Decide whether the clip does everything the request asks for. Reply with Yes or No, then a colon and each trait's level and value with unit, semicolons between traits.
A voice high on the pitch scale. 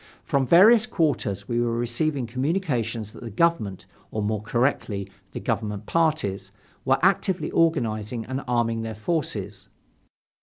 No: low, 120 Hz